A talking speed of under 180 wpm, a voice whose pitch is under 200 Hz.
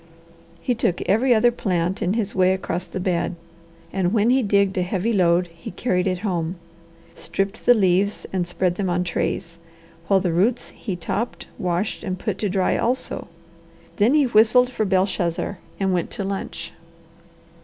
Yes: average, 170 wpm; high, 190 Hz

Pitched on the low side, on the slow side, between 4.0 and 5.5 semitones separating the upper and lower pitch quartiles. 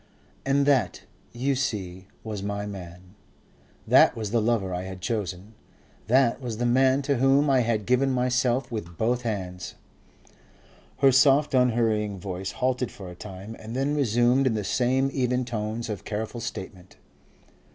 No: low, 115 Hz; average, 155 wpm; average, 4.3 semitones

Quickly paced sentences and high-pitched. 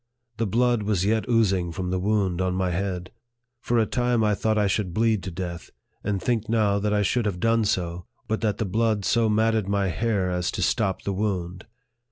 No: fast, 215 wpm; low, 105 Hz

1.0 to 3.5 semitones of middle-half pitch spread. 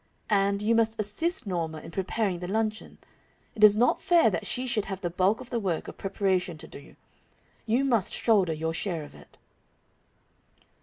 No: average, 3.9 semitones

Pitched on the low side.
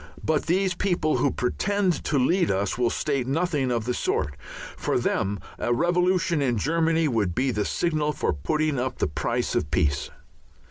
No: medium, 145 Hz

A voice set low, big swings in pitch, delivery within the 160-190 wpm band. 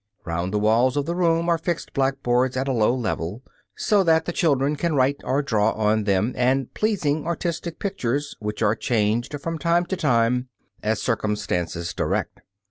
Yes: low, 130 Hz; wide, 6.7 semitones; average, 175 wpm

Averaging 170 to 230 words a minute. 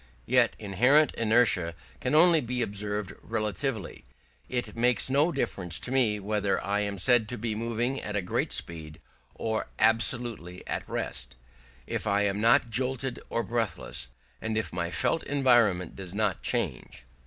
No: average, 155 wpm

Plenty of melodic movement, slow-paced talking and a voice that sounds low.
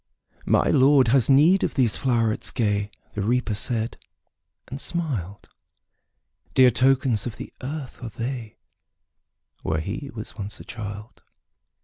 No: average, 3.9 semitones; slow, 130 wpm; low, 120 Hz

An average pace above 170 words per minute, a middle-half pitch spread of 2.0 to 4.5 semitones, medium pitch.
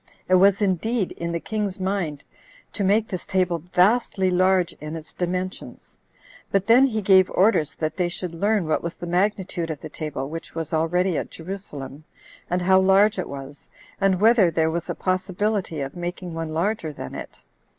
Yes: average, 180 wpm; average, 3.2 semitones; medium, 180 Hz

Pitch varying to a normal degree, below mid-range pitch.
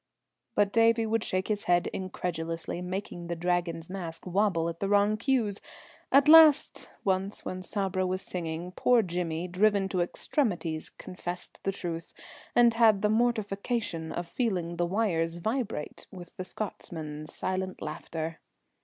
No: average, 3.7 semitones; medium, 185 Hz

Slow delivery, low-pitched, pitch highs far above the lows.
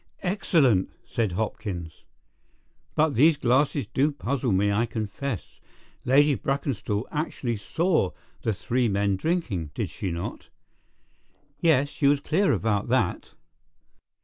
Yes: slow, 120 wpm; low, 125 Hz; wide, 6.2 semitones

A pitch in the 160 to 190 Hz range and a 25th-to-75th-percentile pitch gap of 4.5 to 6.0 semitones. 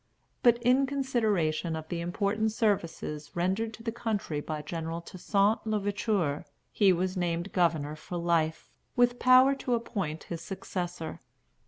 Yes: medium, 185 Hz; average, 5.0 semitones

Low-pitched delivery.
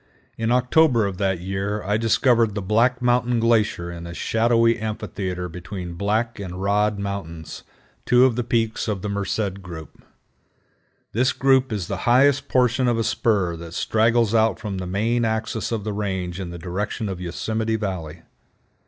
Yes: low, 105 Hz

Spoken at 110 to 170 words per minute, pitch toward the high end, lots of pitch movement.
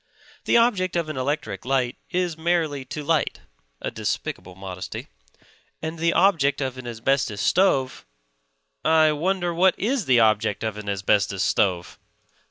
No: average, 145 wpm; medium, 140 Hz; wide, 7.3 semitones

